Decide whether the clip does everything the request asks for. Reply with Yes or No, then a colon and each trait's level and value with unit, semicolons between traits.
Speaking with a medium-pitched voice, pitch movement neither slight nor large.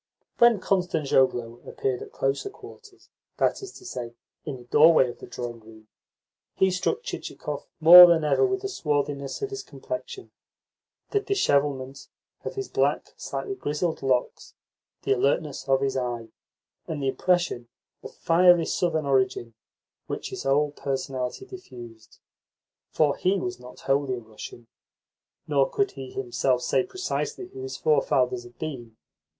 No: medium, 145 Hz; wide, 6.9 semitones